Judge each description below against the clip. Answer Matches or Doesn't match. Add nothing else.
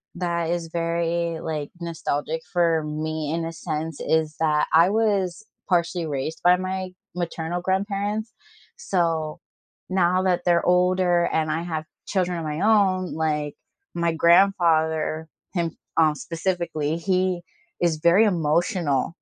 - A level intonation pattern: Matches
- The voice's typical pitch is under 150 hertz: Doesn't match